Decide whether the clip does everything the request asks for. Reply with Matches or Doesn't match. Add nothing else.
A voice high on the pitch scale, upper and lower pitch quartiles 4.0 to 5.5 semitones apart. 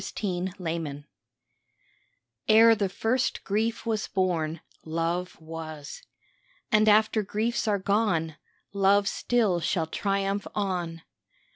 Matches